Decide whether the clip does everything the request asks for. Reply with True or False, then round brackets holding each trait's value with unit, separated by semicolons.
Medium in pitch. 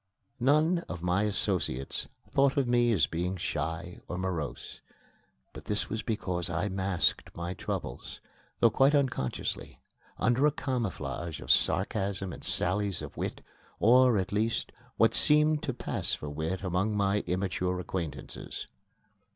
False (95 Hz)